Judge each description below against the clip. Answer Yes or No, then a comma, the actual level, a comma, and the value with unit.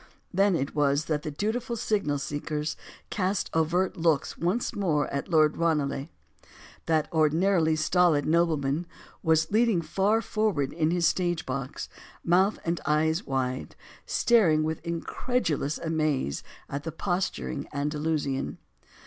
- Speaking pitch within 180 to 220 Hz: No, medium, 160 Hz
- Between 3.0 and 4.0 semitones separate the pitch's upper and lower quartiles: Yes, average, 3.4 semitones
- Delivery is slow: Yes, slow, 125 wpm